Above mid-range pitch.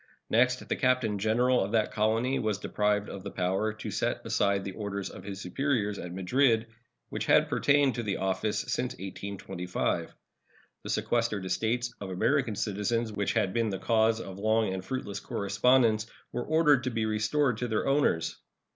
No: low, 110 Hz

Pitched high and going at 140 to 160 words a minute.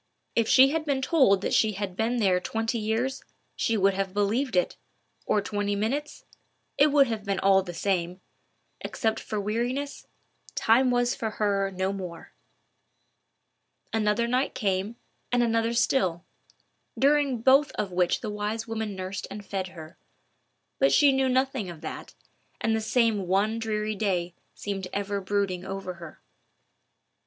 Yes: high, 210 Hz; average, 150 wpm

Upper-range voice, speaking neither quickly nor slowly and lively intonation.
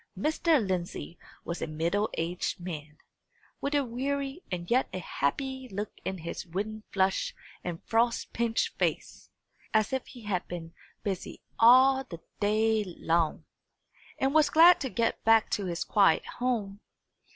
Yes: high, 210 Hz; average, 150 wpm; wide, 6.2 semitones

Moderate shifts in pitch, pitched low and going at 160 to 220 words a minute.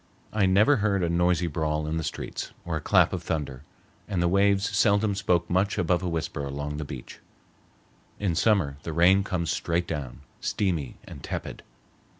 Yes: average, 4.2 semitones; very low, 85 Hz; average, 175 wpm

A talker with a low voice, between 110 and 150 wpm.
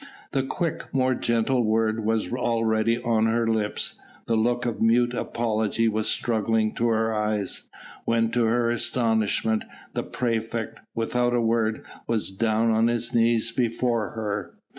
Yes: low, 115 Hz; average, 145 wpm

